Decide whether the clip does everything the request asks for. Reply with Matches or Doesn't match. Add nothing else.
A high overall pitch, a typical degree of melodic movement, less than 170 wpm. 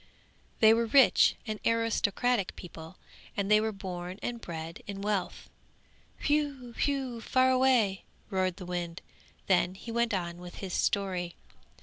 Matches